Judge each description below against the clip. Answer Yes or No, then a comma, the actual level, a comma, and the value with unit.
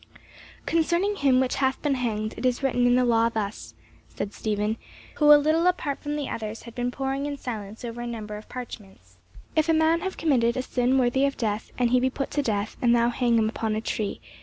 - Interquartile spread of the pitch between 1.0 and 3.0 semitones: No, average, 3.9 semitones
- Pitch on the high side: Yes, high, 245 Hz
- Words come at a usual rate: No, fast, 230 wpm